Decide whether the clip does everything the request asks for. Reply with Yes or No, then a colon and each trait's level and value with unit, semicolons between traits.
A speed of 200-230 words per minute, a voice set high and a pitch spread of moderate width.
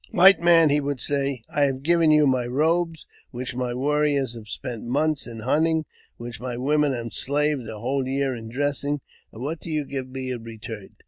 No: fast, 205 wpm; low, 135 Hz; average, 3.4 semitones